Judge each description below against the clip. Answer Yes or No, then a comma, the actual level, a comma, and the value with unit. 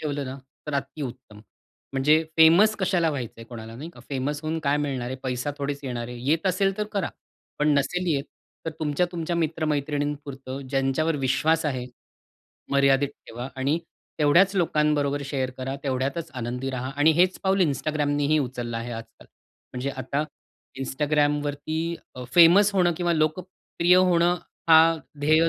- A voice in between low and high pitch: Yes, medium, 145 Hz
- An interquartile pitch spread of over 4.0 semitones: No, average, 3.5 semitones